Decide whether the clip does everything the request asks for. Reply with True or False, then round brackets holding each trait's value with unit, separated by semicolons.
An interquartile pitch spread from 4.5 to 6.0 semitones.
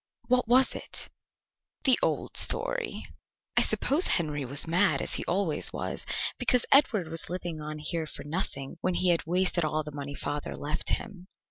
True (5.1 semitones)